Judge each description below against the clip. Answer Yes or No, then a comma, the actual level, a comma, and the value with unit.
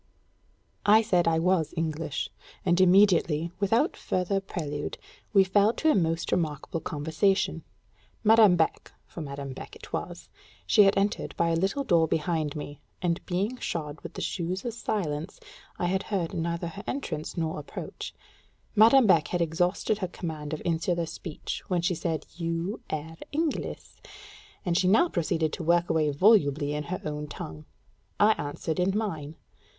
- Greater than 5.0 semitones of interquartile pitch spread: No, average, 3.7 semitones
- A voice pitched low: No, medium, 170 Hz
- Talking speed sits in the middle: Yes, average, 160 wpm